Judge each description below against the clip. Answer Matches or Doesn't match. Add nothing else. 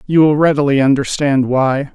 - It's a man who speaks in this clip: Matches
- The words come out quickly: Doesn't match